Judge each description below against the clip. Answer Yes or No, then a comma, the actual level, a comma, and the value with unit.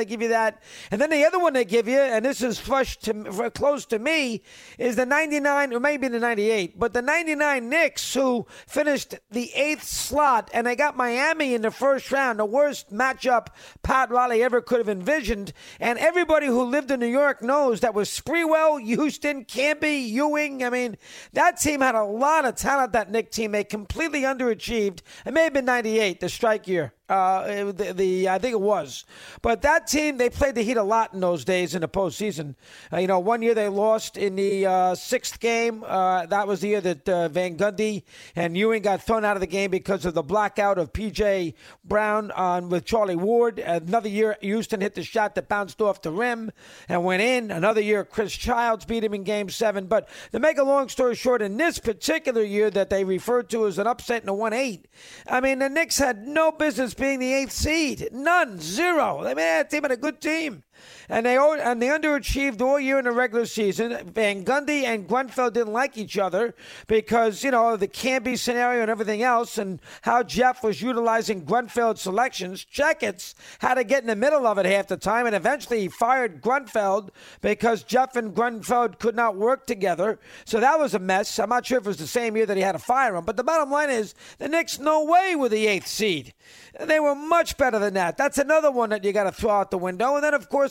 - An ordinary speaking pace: No, fast, 220 wpm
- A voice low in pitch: No, high, 235 Hz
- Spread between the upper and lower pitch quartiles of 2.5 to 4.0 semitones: No, average, 4.7 semitones